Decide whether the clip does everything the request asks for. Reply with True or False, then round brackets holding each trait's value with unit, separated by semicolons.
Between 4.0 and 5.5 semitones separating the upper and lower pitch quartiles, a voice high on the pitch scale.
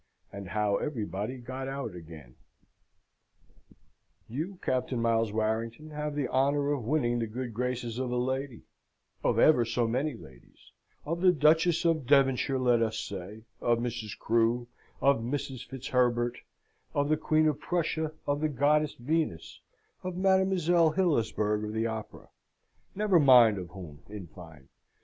False (5.1 semitones; 125 Hz)